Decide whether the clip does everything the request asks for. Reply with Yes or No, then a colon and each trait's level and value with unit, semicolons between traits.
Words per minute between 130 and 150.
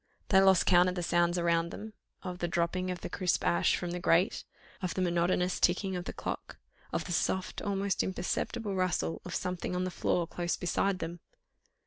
No: average, 190 wpm